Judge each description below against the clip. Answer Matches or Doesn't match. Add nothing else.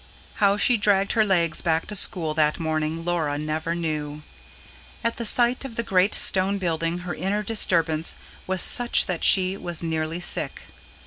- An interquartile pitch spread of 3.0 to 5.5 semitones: Matches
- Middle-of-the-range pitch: Matches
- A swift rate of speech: Doesn't match